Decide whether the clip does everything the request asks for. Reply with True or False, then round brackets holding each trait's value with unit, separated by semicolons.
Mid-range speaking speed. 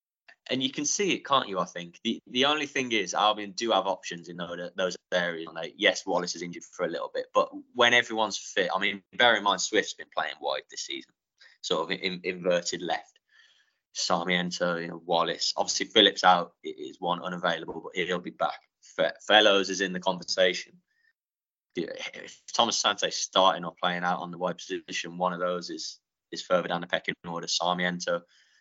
True (195 wpm)